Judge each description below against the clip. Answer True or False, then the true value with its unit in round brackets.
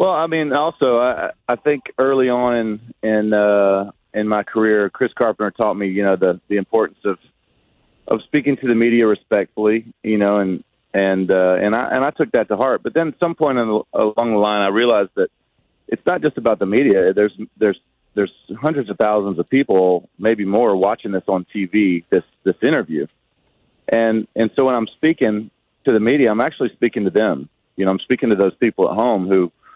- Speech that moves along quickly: True (210 wpm)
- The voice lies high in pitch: False (105 Hz)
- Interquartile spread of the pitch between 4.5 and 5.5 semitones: False (3.6 semitones)